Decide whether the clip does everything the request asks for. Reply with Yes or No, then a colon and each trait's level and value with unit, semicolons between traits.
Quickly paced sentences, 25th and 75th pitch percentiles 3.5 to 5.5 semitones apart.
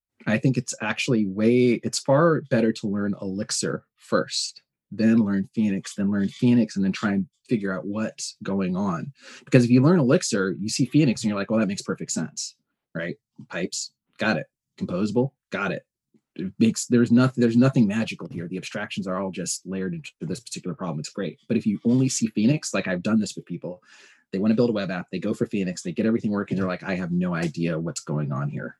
Yes: fast, 225 wpm; average, 4.5 semitones